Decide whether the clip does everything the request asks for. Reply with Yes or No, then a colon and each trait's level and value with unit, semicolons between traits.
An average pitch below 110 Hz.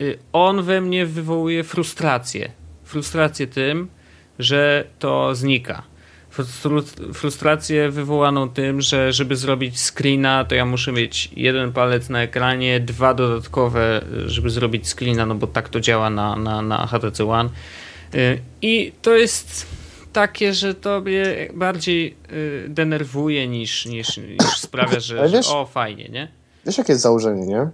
No: low, 130 Hz